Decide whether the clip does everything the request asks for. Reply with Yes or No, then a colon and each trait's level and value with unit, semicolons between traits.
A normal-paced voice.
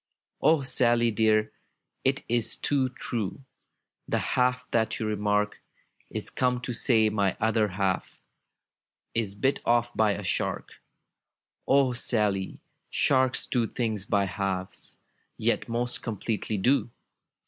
No: slow, 125 wpm